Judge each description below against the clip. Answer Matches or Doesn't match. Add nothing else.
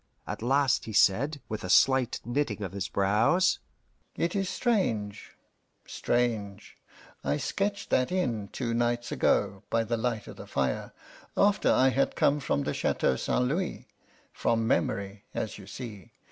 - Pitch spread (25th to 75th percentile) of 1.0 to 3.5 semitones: Doesn't match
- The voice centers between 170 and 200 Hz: Doesn't match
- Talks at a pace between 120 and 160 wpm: Matches